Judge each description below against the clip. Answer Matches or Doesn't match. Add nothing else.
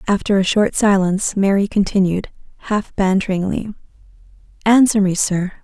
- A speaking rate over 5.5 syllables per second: Doesn't match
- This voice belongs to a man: Doesn't match